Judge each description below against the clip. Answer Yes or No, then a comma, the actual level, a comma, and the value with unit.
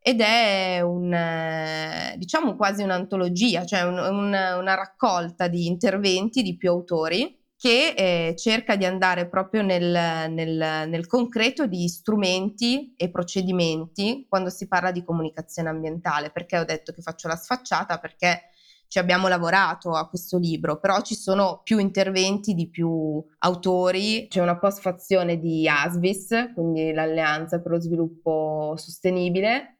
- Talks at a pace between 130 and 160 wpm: Yes, average, 140 wpm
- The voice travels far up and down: No, average, 2.9 semitones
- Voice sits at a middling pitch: Yes, medium, 180 Hz